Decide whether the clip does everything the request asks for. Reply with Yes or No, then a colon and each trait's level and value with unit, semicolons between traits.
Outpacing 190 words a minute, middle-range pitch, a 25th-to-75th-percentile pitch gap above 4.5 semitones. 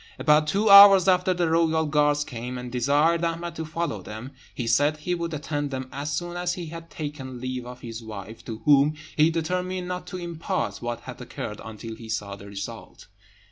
Yes: average, 200 wpm; medium, 150 Hz; wide, 5.6 semitones